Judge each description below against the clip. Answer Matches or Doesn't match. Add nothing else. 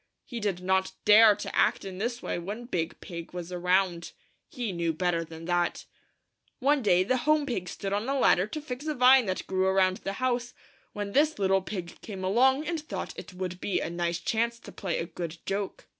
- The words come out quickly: Matches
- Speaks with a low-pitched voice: Doesn't match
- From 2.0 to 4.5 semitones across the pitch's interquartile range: Doesn't match